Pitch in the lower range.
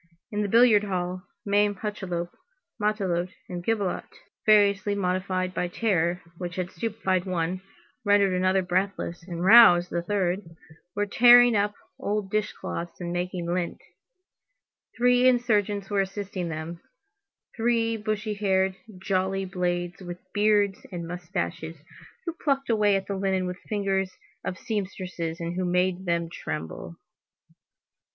No: high, 190 Hz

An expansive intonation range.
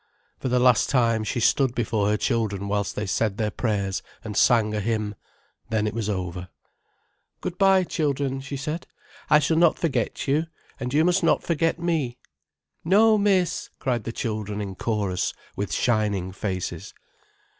Yes: wide, 6.3 semitones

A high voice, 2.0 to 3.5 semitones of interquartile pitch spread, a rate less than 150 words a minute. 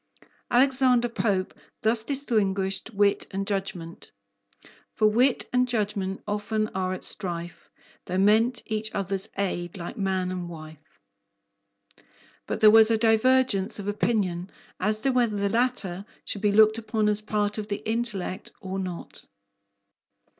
Yes: high, 210 Hz; average, 2.8 semitones; average, 140 wpm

